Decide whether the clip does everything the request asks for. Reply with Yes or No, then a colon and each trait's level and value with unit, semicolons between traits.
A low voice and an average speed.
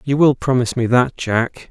No: low, 125 Hz; fast, 210 wpm